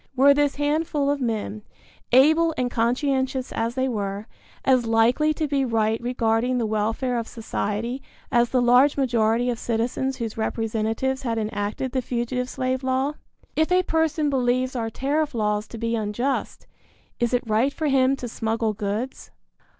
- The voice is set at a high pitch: Yes, high, 245 Hz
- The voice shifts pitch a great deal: No, average, 3.0 semitones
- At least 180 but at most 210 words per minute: No, average, 160 wpm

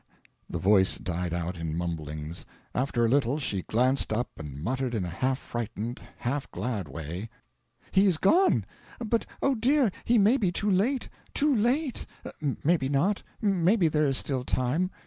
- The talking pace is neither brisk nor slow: Yes, average, 165 wpm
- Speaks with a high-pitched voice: No, low, 130 Hz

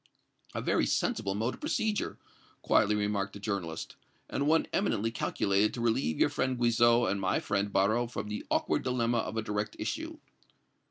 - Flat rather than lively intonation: No, average, 3.2 semitones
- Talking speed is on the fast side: No, average, 170 wpm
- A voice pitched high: No, low, 110 Hz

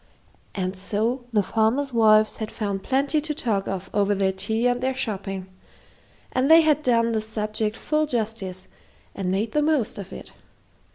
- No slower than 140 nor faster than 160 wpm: No, average, 170 wpm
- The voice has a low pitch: No, high, 220 Hz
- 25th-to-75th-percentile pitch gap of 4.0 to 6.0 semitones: Yes, average, 4.4 semitones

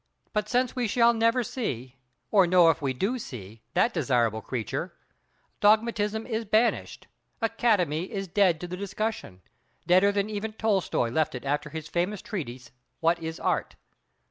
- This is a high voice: Yes, high, 195 Hz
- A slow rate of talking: No, average, 150 wpm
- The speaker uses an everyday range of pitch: No, wide, 6.4 semitones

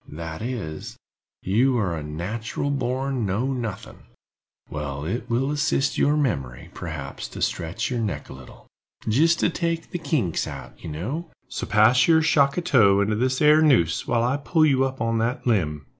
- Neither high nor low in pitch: No, low, 120 Hz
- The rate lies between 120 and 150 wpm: No, average, 180 wpm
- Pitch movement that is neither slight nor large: No, wide, 7.7 semitones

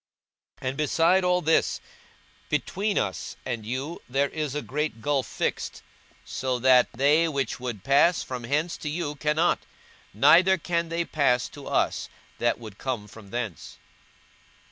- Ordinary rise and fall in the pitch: Yes, average, 4.7 semitones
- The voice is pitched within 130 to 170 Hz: Yes, medium, 140 Hz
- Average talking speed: Yes, average, 150 wpm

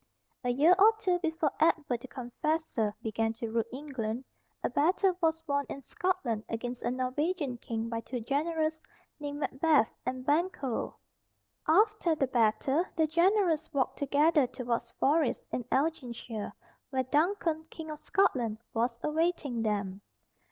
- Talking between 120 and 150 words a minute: Yes, average, 140 wpm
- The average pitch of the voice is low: No, very high, 285 Hz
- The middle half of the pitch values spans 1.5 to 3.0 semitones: No, average, 5.1 semitones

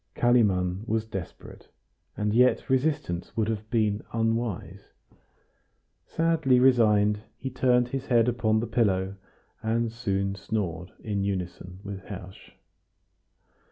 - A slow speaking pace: Yes, slow, 115 wpm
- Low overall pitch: Yes, low, 110 Hz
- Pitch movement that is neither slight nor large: Yes, average, 3.6 semitones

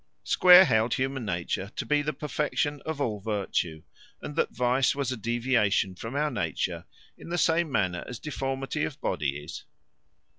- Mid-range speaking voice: No, low, 125 Hz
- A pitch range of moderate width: No, wide, 6.7 semitones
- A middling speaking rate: Yes, average, 170 wpm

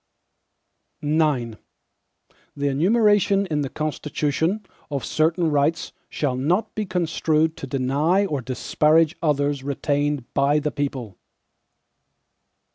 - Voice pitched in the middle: Yes, medium, 150 Hz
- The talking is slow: Yes, slow, 105 wpm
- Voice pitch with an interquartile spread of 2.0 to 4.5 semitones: Yes, average, 2.7 semitones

